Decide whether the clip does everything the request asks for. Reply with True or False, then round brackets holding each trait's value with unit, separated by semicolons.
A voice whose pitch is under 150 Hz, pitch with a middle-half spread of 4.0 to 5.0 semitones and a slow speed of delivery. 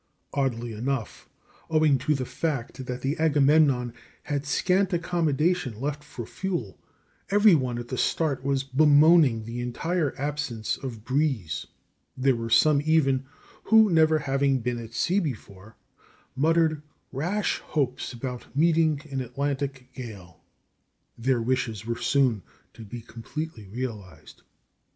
True (135 Hz; 4.4 semitones; 130 wpm)